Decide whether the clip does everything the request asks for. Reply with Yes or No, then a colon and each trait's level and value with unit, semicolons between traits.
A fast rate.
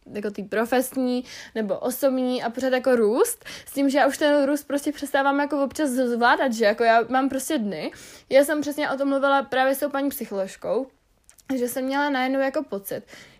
Yes: fast, 195 wpm